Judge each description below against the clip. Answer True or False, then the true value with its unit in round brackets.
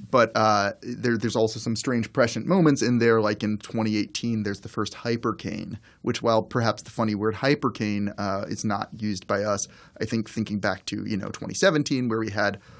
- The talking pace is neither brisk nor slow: True (195 wpm)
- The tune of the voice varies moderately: False (2.0 semitones)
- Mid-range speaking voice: False (110 Hz)